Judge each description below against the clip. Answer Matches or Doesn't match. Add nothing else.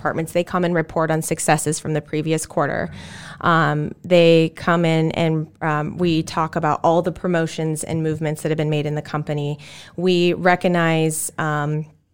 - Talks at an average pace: Matches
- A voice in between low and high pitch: Matches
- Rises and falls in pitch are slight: Matches